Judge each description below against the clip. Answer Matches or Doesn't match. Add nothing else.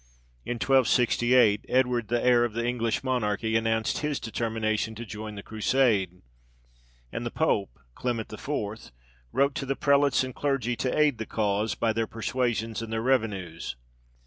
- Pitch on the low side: Matches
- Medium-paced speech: Matches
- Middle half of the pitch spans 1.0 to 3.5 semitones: Matches